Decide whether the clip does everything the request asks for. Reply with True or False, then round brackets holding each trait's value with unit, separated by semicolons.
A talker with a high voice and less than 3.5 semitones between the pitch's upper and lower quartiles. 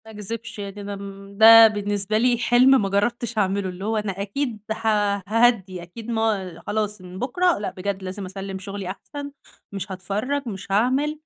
True (205 Hz; 2.8 semitones)